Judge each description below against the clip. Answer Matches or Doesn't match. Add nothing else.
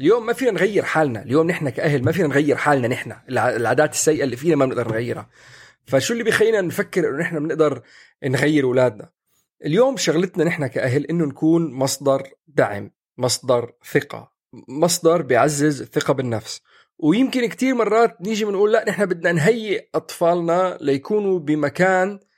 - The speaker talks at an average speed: Doesn't match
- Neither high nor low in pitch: Matches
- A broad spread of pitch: Matches